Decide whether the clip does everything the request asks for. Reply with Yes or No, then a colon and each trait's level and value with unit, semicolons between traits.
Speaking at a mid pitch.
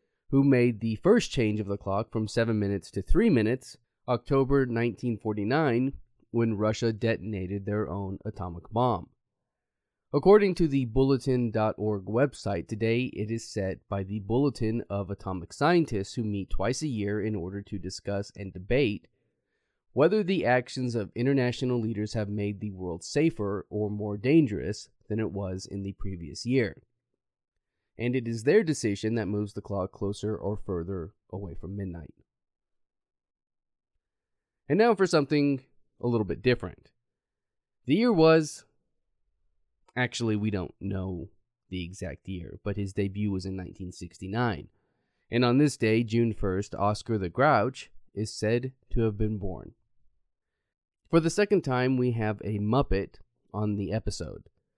No: low, 105 Hz